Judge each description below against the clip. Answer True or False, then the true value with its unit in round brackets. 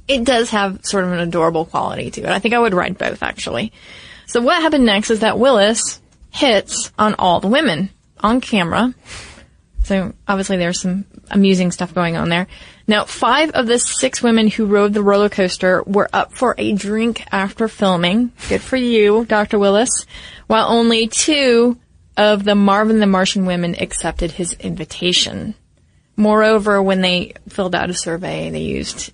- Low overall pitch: False (205 Hz)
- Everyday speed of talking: True (175 wpm)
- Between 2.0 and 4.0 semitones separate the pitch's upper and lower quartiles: True (3.7 semitones)